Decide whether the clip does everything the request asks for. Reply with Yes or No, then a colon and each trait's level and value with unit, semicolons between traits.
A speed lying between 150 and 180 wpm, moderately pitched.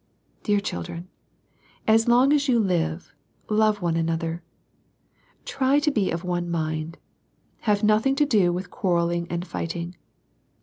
No: slow, 135 wpm; medium, 180 Hz